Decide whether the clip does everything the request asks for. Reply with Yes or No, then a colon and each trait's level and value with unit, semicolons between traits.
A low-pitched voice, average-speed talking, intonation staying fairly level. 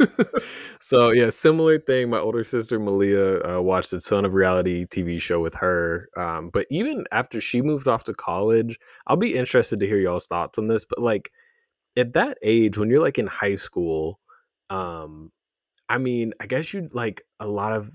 No: low, 110 Hz; average, 190 wpm; average, 4.7 semitones